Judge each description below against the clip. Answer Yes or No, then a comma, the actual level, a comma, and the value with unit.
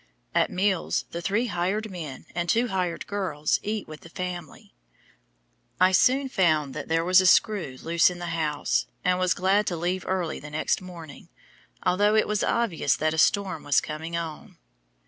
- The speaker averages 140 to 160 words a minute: No, average, 180 wpm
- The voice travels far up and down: No, average, 3.3 semitones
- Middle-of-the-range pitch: Yes, medium, 180 Hz